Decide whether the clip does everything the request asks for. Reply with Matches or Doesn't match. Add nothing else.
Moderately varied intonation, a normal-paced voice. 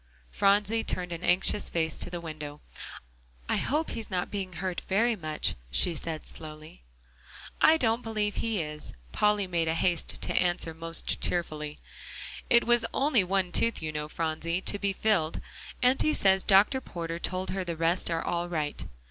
Matches